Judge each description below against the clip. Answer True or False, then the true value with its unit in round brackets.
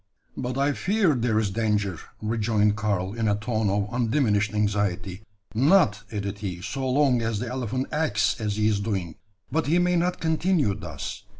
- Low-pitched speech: True (110 Hz)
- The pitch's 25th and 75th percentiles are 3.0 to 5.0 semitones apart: True (4.4 semitones)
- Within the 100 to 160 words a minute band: False (175 wpm)